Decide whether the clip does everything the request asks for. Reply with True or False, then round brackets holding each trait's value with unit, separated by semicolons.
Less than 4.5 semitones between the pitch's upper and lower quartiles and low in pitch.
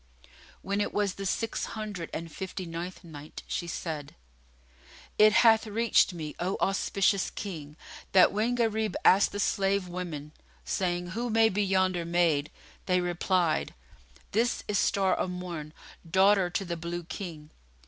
False (3.2 semitones; 185 Hz)